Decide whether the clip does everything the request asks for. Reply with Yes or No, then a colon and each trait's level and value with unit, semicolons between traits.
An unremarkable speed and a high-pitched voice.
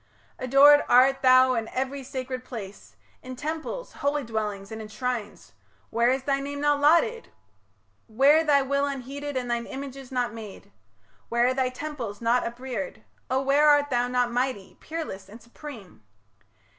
Yes: average, 155 wpm; very high, 255 Hz